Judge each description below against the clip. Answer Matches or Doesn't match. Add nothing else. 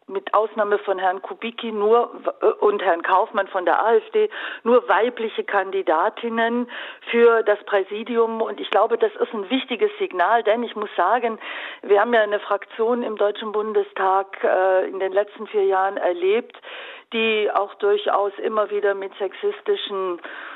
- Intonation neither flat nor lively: Matches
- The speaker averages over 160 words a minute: Doesn't match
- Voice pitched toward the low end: Doesn't match